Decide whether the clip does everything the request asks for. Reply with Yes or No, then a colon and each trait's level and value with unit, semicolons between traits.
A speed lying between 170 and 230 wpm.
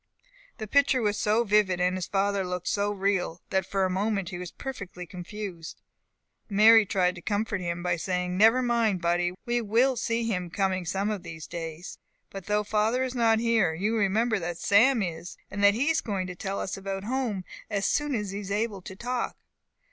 Yes: average, 200 wpm